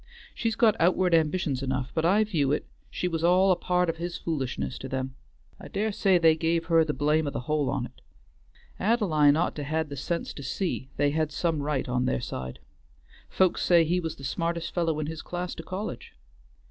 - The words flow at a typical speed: No, fast, 210 wpm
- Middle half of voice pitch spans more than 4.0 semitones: No, average, 3.7 semitones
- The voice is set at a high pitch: No, medium, 160 Hz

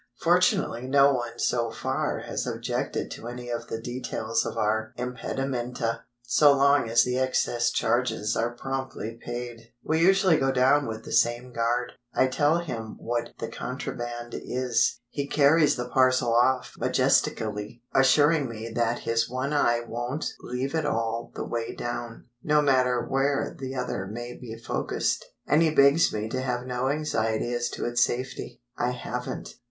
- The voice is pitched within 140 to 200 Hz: No, low, 125 Hz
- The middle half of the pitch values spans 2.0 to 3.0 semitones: Yes, narrow, 2.4 semitones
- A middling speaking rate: Yes, average, 160 wpm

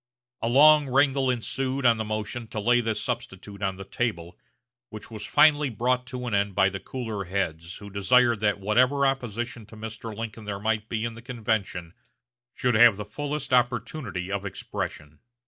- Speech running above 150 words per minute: Yes, average, 175 wpm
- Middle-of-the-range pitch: No, low, 115 Hz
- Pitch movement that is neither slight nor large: Yes, average, 3.7 semitones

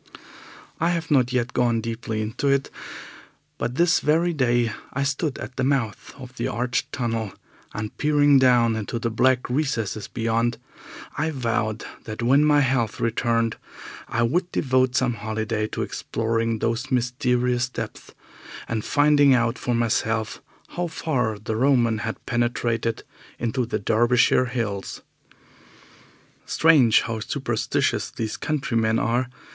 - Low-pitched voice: Yes, low, 120 Hz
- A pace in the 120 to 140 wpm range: Yes, slow, 135 wpm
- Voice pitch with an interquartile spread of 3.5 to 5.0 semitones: No, average, 2.7 semitones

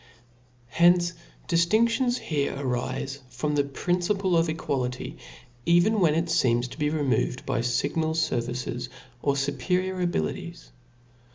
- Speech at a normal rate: No, slow, 115 wpm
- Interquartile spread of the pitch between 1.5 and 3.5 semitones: No, average, 5.3 semitones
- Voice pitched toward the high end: No, medium, 150 Hz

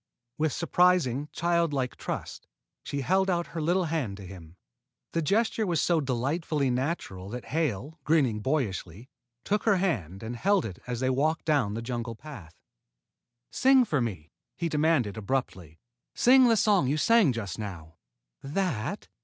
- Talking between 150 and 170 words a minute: Yes, average, 155 wpm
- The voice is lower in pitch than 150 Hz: Yes, medium, 140 Hz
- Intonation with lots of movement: Yes, wide, 7.3 semitones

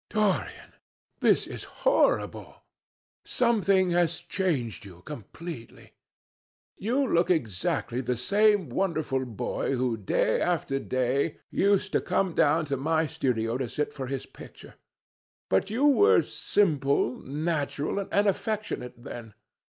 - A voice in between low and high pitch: Yes, medium, 155 Hz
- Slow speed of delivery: Yes, slow, 120 wpm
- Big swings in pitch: Yes, wide, 7.4 semitones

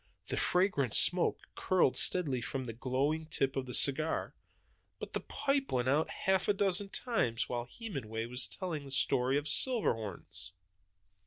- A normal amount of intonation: No, wide, 6.8 semitones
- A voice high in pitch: No, medium, 140 Hz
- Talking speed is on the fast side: No, average, 155 wpm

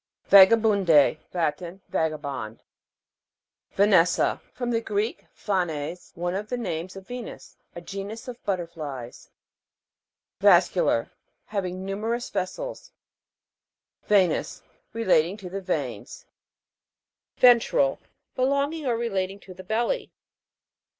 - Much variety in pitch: No, average, 5.0 semitones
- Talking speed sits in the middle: No, slow, 100 wpm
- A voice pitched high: Yes, high, 195 Hz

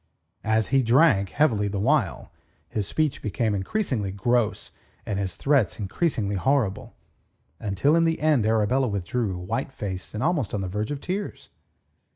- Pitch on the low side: Yes, low, 110 Hz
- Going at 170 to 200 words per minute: No, average, 160 wpm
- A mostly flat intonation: No, wide, 5.5 semitones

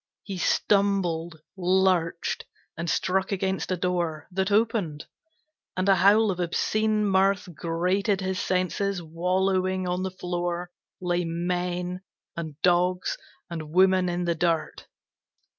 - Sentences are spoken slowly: Yes, slow, 125 wpm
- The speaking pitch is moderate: Yes, medium, 180 Hz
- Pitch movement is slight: Yes, narrow, 1.7 semitones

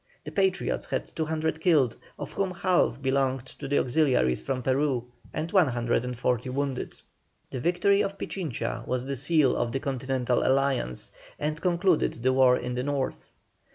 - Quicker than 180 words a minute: No, average, 155 wpm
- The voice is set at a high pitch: No, low, 135 Hz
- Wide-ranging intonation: No, average, 4.2 semitones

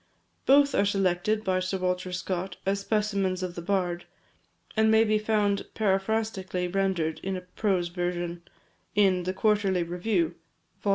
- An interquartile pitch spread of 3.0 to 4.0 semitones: No, narrow, 2.5 semitones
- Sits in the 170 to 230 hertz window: Yes, high, 190 Hz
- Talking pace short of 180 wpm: Yes, average, 150 wpm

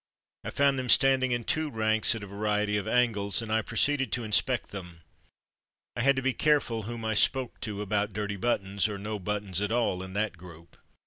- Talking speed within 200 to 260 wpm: Yes, fast, 205 wpm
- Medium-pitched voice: No, low, 110 Hz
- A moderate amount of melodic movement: Yes, average, 3.2 semitones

